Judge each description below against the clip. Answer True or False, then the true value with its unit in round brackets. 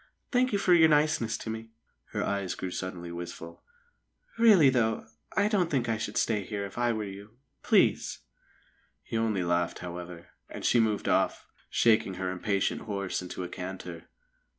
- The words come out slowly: False (170 wpm)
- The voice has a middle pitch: False (105 Hz)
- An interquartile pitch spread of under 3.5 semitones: False (4.6 semitones)